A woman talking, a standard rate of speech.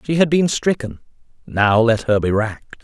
No: male; average, 190 wpm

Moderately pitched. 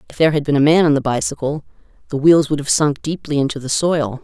Yes: medium, 145 Hz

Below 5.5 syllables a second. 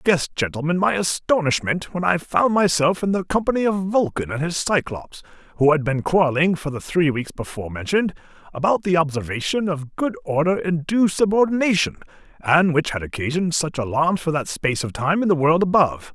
No: 5.6 syllables/s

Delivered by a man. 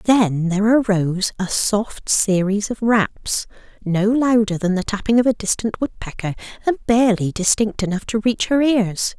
No: female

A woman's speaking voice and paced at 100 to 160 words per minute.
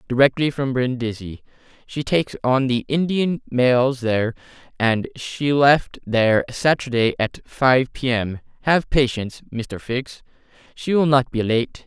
No: male; slow, 135 wpm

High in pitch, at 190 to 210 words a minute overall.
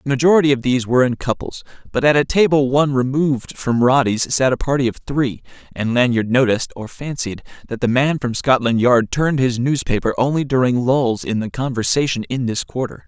No: low, 130 Hz; average, 195 wpm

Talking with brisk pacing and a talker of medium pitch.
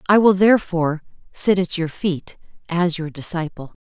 No: average, 155 wpm; medium, 175 Hz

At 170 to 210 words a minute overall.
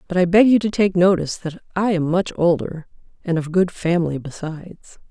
Yes: average, 200 wpm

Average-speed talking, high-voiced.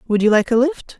No: fast, 300 wpm; high, 245 Hz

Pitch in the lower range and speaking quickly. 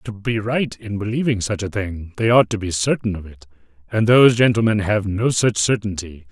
Yes: low, 105 Hz; fast, 210 wpm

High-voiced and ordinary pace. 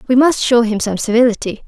No: high, 240 Hz; fast, 215 wpm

